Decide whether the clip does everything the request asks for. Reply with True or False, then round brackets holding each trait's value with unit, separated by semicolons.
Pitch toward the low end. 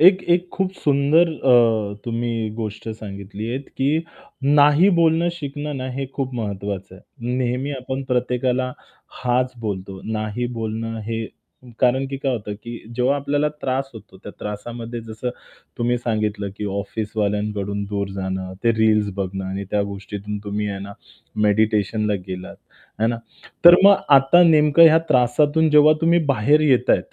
True (120 Hz)